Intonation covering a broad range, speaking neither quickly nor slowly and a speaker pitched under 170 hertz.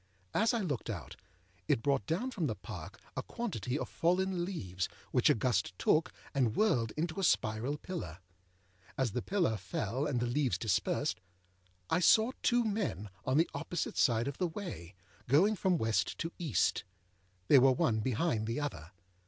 Yes: wide, 8.1 semitones; average, 170 wpm; medium, 140 Hz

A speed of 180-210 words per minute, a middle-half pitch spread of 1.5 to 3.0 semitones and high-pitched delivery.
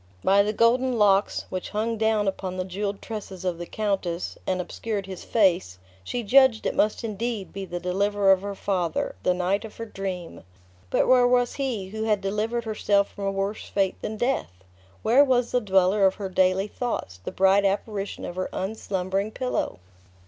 Yes: average, 185 wpm; average, 2.7 semitones; high, 200 Hz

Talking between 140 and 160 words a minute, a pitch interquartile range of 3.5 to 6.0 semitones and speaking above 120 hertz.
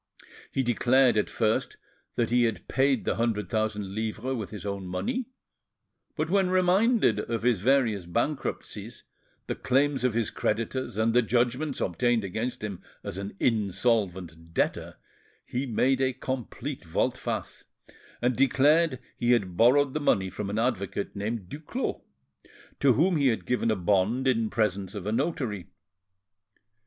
No: average, 150 wpm; average, 4.4 semitones; low, 115 Hz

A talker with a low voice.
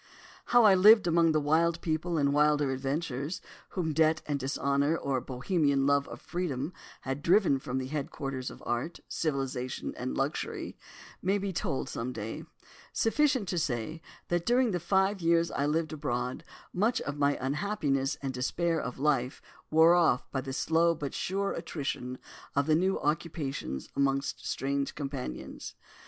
No: medium, 150 Hz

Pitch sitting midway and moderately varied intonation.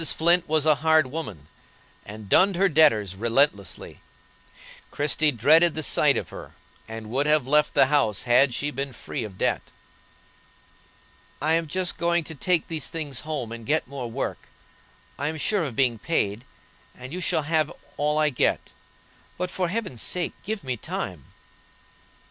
Yes: medium, 150 Hz; average, 4.8 semitones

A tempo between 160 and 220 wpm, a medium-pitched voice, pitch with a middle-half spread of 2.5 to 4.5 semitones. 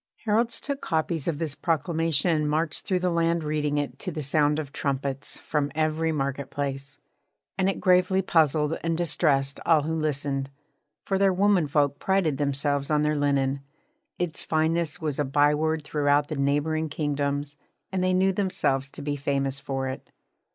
Yes: average, 170 wpm; medium, 150 Hz; average, 2.8 semitones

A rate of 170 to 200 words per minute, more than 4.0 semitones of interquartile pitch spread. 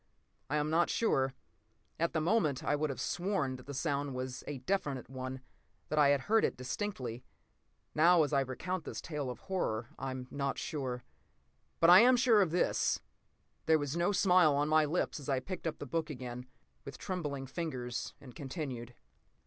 Yes: average, 190 wpm; average, 4.7 semitones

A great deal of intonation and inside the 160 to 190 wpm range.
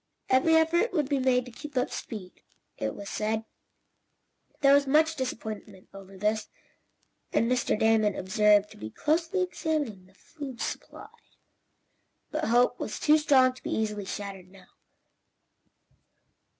No: wide, 6.1 semitones; average, 145 wpm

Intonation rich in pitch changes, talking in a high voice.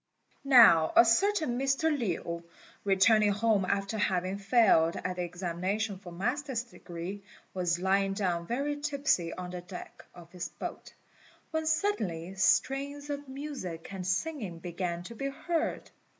Yes: wide, 7.3 semitones; high, 195 Hz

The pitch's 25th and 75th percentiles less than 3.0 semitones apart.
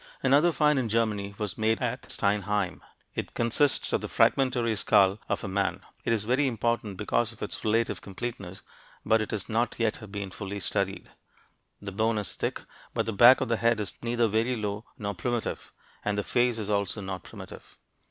Yes: narrow, 2.6 semitones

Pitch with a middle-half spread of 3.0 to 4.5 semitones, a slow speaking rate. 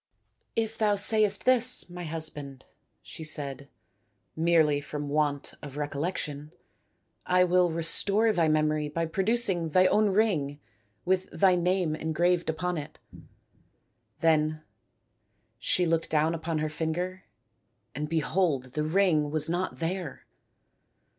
Yes: average, 3.3 semitones; slow, 130 wpm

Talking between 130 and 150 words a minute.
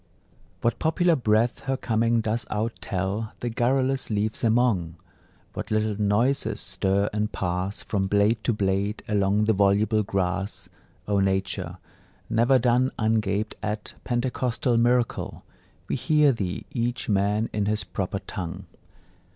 Yes: slow, 135 wpm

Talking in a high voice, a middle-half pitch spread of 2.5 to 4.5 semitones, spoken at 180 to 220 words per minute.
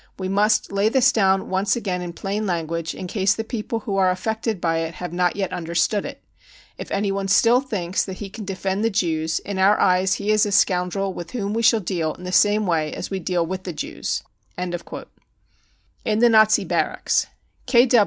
Yes: high, 195 Hz; average, 2.9 semitones; fast, 205 wpm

